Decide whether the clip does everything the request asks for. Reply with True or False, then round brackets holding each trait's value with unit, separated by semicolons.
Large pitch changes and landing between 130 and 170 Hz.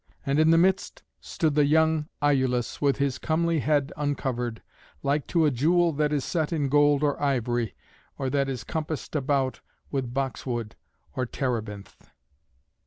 False (2.9 semitones; 140 Hz)